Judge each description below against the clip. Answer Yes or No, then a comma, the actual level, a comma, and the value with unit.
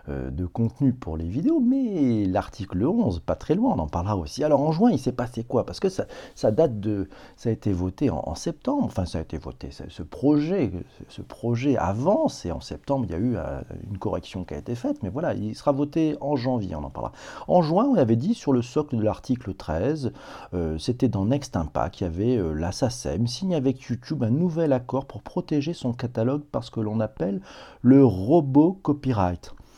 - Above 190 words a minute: Yes, fast, 220 wpm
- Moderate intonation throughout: No, wide, 7.5 semitones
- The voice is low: Yes, low, 120 Hz